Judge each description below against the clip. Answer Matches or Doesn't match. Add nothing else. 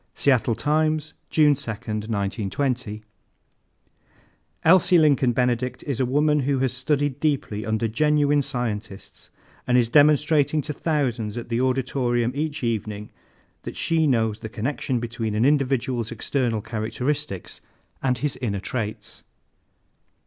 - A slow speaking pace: Matches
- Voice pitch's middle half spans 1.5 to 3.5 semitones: Doesn't match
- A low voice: Matches